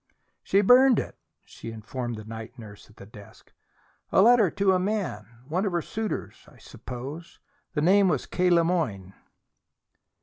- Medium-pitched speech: Yes, medium, 165 Hz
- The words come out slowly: No, average, 165 wpm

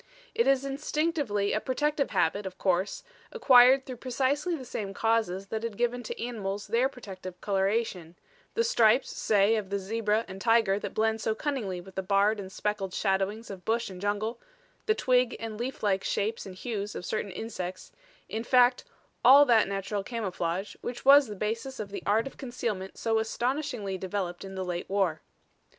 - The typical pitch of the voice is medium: No, high, 215 Hz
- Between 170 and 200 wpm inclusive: Yes, average, 175 wpm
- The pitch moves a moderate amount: Yes, average, 4.0 semitones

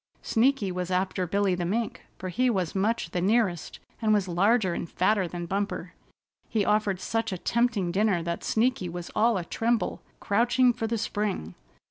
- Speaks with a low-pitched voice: No, high, 200 Hz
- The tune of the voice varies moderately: Yes, average, 3.9 semitones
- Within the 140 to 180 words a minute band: Yes, average, 170 wpm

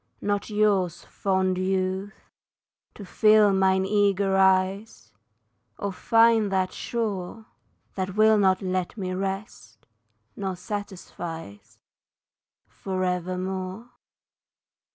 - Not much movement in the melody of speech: Yes, narrow, 1.7 semitones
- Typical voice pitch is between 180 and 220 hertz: Yes, high, 190 Hz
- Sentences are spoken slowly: Yes, slow, 90 wpm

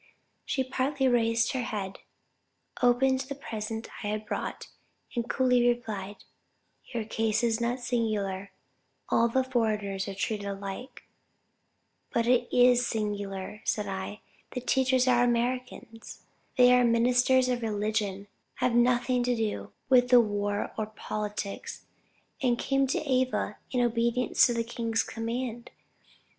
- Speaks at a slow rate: Yes, slow, 130 wpm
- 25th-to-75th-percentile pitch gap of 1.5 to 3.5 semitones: Yes, average, 2.8 semitones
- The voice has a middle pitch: No, high, 235 Hz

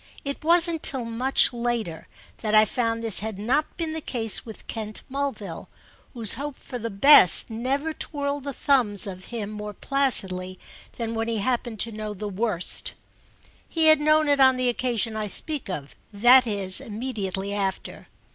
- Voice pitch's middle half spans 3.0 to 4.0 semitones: No, average, 4.7 semitones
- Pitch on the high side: Yes, high, 230 Hz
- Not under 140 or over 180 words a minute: Yes, average, 165 wpm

